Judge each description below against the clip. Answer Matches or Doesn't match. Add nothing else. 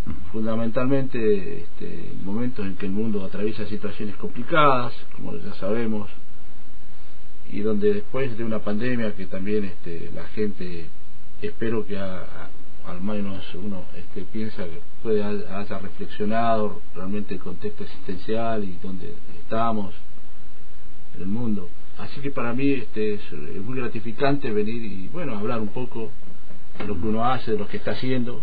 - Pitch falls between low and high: Doesn't match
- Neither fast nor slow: Matches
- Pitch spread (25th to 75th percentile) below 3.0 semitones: Matches